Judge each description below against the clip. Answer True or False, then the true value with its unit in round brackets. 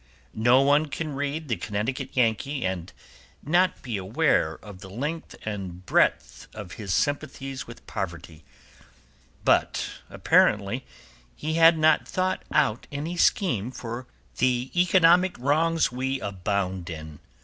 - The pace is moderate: False (130 wpm)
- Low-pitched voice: True (130 Hz)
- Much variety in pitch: True (7.5 semitones)